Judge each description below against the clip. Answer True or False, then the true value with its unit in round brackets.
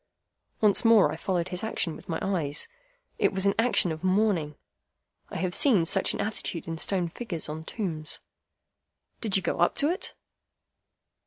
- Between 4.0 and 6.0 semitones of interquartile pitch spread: True (4.3 semitones)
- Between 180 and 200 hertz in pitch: True (185 Hz)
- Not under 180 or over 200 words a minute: False (170 wpm)